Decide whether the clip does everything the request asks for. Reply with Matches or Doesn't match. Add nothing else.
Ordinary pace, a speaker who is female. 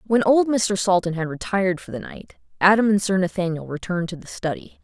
Doesn't match